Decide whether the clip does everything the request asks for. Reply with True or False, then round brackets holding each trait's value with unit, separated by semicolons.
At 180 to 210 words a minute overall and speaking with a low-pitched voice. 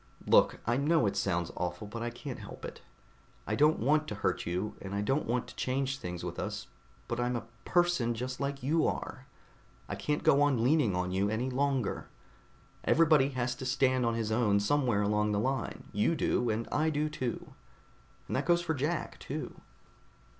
True (195 wpm; 125 Hz)